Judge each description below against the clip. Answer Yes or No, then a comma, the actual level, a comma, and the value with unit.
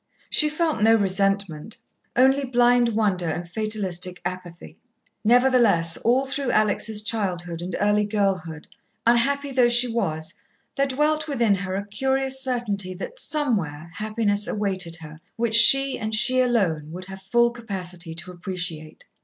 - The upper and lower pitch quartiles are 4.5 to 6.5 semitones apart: Yes, average, 5.1 semitones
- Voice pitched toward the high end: Yes, high, 210 Hz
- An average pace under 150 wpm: Yes, average, 140 wpm